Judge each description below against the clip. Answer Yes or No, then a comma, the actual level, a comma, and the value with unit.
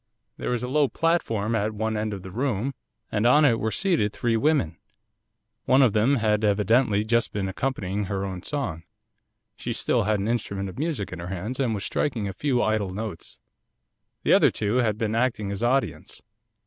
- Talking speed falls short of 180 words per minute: No, average, 195 wpm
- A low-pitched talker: Yes, low, 110 Hz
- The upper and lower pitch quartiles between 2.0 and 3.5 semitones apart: No, average, 3.9 semitones